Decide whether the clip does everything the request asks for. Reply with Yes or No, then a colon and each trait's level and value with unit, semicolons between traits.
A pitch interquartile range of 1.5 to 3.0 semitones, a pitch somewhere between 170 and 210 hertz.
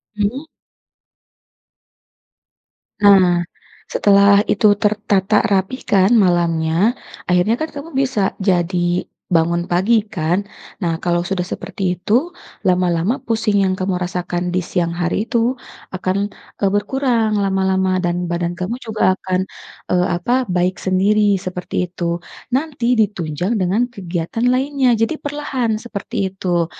No: average, 3.8 semitones; high, 190 Hz